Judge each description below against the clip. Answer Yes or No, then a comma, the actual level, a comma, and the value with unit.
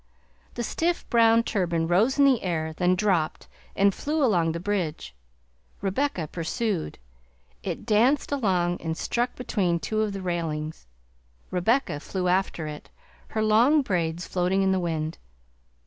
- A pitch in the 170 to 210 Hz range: Yes, medium, 185 Hz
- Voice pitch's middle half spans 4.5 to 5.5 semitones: Yes, average, 5.2 semitones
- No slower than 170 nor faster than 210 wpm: No, average, 145 wpm